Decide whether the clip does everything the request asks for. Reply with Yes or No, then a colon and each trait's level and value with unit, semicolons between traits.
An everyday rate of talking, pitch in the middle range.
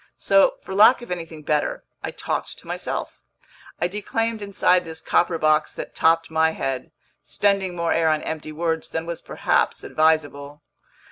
Yes: average, 160 wpm; medium, 165 Hz